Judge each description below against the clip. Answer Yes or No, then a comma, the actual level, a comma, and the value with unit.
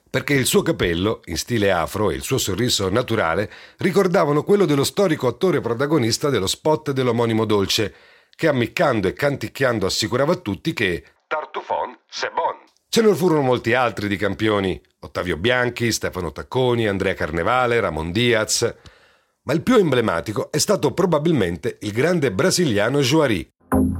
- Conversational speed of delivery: Yes, average, 150 wpm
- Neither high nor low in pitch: No, low, 125 Hz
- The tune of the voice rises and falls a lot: Yes, wide, 6.5 semitones